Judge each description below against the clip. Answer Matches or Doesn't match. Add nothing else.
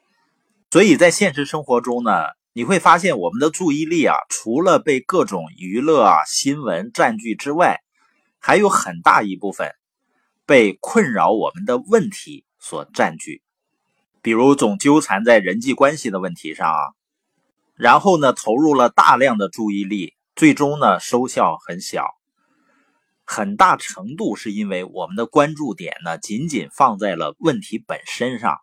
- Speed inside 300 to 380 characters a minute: Doesn't match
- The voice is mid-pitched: Matches